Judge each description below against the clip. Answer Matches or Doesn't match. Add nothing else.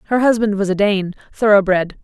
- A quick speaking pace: Doesn't match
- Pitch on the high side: Matches